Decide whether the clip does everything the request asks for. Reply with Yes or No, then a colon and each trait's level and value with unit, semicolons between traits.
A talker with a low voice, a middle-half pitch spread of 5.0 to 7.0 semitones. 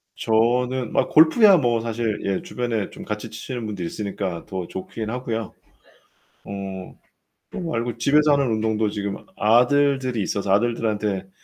No: low, 115 Hz; average, 3.4 semitones